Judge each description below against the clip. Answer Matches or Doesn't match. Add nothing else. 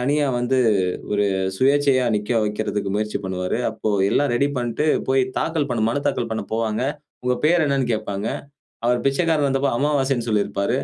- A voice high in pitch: Doesn't match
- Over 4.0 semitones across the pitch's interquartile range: Matches